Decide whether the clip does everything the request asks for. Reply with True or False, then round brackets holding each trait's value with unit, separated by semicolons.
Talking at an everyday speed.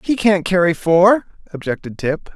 True (155 wpm)